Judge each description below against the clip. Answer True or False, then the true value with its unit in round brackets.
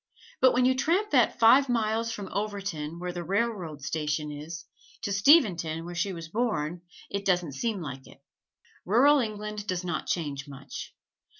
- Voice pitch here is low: False (195 Hz)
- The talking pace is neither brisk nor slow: True (165 wpm)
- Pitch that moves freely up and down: True (5.8 semitones)